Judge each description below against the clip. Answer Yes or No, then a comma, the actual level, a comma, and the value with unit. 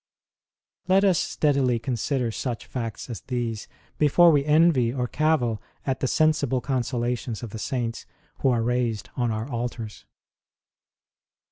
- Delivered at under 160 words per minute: Yes, average, 140 wpm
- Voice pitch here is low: Yes, low, 125 Hz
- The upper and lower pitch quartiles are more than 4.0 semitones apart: No, average, 3.4 semitones